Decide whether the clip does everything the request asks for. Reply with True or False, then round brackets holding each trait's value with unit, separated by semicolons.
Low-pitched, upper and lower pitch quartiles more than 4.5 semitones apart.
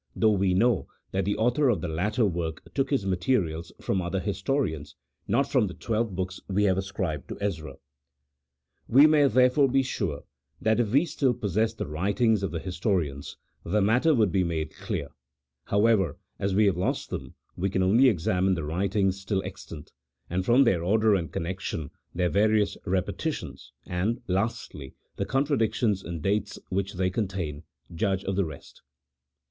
False (95 Hz; 3.9 semitones)